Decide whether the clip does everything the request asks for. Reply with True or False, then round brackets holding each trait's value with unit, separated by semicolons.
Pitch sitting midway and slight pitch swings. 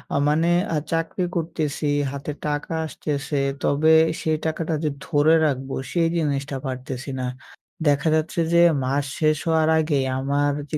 True (150 Hz; 2.2 semitones)